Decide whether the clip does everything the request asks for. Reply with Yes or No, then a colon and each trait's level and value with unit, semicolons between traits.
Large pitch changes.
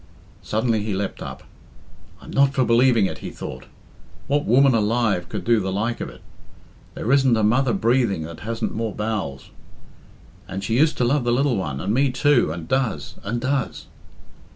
No: average, 4.3 semitones